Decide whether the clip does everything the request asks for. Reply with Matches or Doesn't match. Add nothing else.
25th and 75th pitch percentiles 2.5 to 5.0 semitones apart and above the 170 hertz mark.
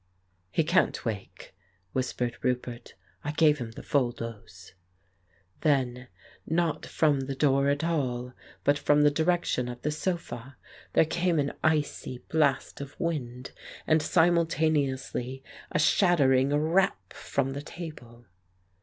Doesn't match